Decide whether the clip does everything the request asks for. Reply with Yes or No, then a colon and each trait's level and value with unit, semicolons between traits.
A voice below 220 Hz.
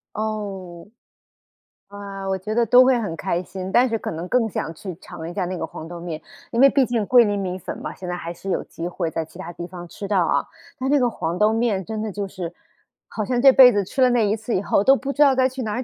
Yes: high, 205 Hz